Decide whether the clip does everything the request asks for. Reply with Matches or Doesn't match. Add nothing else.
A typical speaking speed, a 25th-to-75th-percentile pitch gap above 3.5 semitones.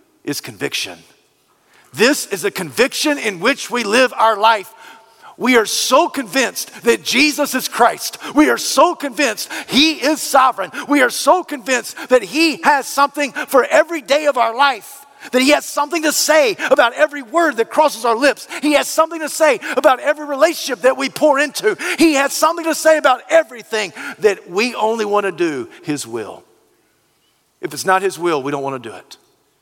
Matches